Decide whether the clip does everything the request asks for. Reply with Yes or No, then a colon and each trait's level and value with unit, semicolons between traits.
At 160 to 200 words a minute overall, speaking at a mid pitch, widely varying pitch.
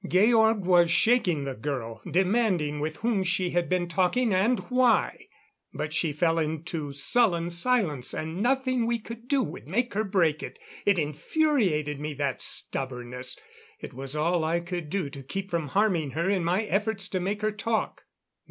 Yes: average, 170 wpm; medium, 175 Hz; wide, 6.1 semitones